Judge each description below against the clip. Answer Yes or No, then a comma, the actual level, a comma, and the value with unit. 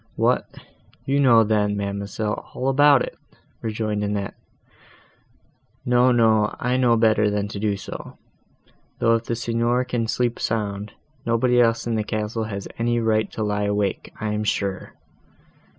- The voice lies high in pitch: No, low, 110 Hz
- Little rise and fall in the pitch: Yes, narrow, 2.3 semitones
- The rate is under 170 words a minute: Yes, average, 155 wpm